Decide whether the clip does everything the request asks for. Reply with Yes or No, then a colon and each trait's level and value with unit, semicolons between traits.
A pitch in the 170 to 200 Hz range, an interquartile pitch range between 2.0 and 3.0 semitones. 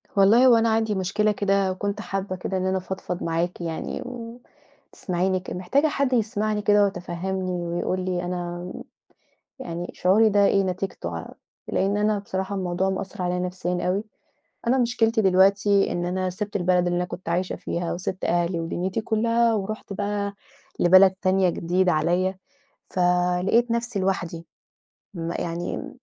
Yes: high, 190 Hz; narrow, 2.6 semitones